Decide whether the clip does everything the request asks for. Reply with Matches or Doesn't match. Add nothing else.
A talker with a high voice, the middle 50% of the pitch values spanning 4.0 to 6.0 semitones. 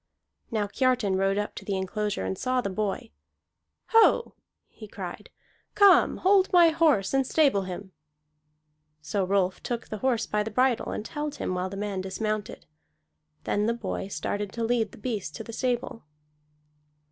Matches